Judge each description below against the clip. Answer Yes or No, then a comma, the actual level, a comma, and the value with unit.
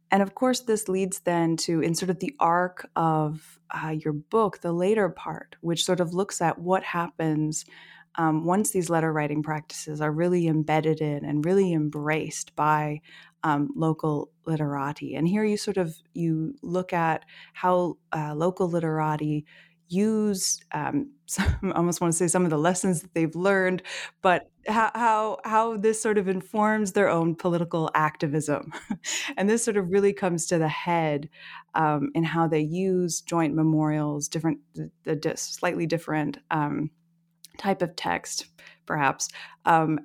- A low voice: No, medium, 165 Hz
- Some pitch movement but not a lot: Yes, average, 3.3 semitones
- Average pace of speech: Yes, average, 160 wpm